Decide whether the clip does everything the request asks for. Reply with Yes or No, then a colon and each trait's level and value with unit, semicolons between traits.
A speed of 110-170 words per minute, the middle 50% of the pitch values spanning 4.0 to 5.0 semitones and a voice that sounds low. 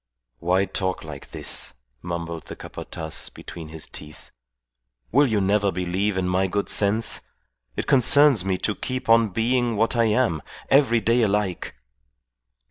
Yes: average, 145 wpm; average, 4.4 semitones; low, 100 Hz